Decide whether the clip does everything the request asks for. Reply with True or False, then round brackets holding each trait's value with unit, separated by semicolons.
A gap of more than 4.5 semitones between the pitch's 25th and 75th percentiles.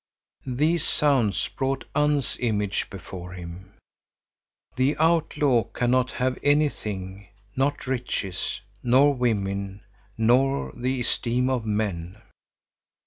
True (5.4 semitones)